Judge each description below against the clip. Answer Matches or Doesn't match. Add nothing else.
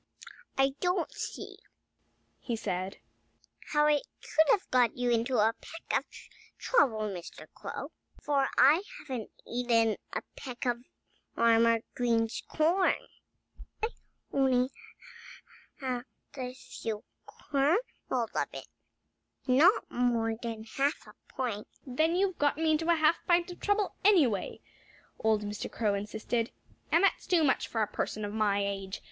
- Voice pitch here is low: Doesn't match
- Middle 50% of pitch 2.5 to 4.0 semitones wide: Doesn't match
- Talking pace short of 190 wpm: Matches